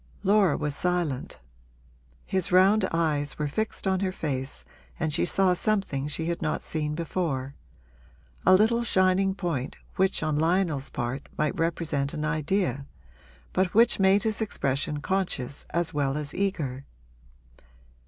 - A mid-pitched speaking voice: Yes, medium, 165 Hz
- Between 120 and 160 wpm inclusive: Yes, average, 140 wpm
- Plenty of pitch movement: No, average, 4.7 semitones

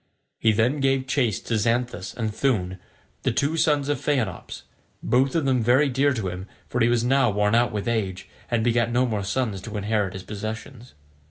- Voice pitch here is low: Yes, low, 120 Hz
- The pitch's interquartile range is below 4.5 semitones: Yes, average, 3.9 semitones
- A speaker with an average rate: Yes, average, 195 wpm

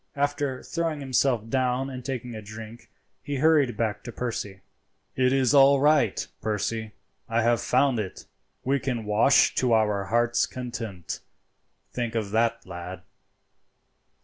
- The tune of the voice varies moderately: Yes, average, 3.4 semitones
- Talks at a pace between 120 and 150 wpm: Yes, average, 140 wpm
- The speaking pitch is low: Yes, low, 120 Hz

